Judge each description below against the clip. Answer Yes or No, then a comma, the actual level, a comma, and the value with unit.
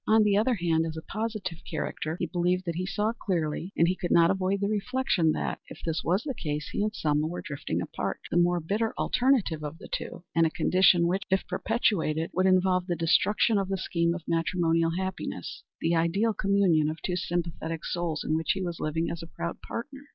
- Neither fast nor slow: No, fast, 215 wpm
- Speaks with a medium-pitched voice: Yes, medium, 175 Hz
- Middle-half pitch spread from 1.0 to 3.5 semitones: Yes, average, 3.2 semitones